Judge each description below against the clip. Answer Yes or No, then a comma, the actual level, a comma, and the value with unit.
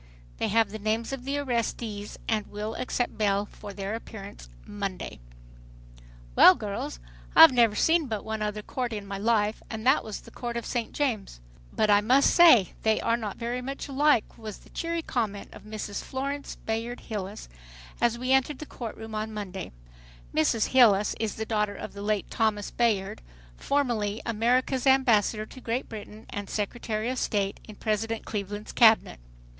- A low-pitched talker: No, high, 220 Hz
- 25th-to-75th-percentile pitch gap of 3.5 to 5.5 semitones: No, average, 2.9 semitones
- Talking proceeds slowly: No, average, 175 wpm